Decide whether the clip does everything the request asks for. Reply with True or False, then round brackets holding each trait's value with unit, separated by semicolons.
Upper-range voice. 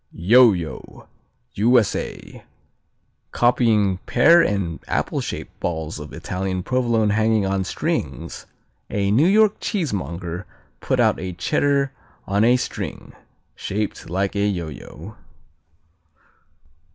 False (105 Hz)